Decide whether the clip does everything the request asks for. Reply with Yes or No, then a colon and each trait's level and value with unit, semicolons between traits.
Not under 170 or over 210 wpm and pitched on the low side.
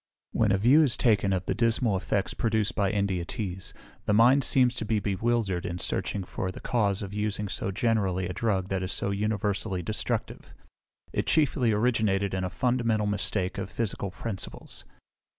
Yes: average, 175 wpm; low, 105 Hz